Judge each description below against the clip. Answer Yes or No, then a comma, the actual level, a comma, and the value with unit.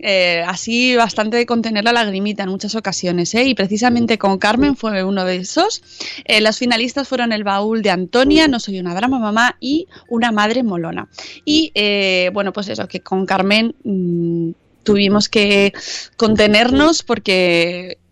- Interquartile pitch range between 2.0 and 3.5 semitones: No, average, 3.9 semitones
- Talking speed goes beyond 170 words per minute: No, average, 160 wpm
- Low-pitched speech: No, high, 210 Hz